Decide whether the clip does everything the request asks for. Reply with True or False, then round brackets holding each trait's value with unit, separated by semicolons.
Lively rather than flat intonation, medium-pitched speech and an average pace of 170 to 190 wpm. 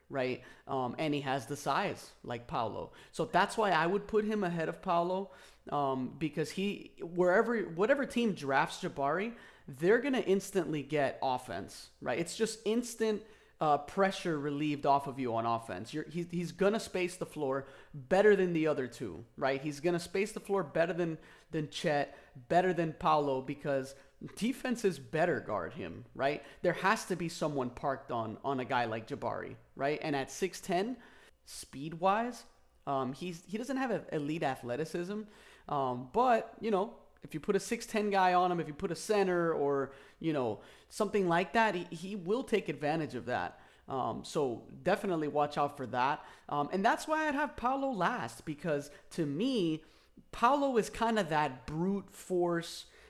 True (5.9 semitones; 170 Hz; 175 wpm)